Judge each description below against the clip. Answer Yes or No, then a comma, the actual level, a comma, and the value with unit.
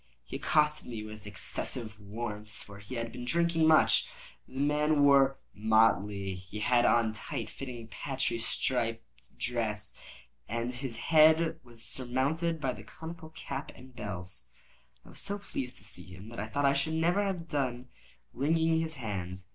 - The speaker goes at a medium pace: Yes, average, 165 wpm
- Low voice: Yes, low, 125 Hz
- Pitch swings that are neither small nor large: No, wide, 5.9 semitones